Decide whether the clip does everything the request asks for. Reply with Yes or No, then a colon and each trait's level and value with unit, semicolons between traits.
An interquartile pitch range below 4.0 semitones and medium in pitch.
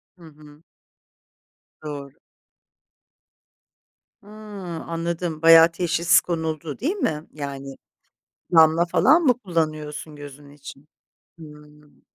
Yes: narrow, 2.4 semitones; medium, 155 Hz